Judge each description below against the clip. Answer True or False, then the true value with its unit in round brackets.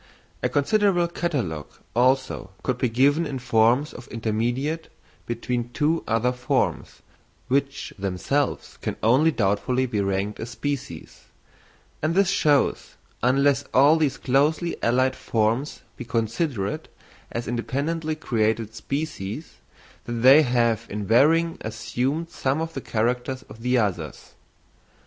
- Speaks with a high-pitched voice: False (125 Hz)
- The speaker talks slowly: True (120 wpm)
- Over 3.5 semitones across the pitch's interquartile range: True (4.3 semitones)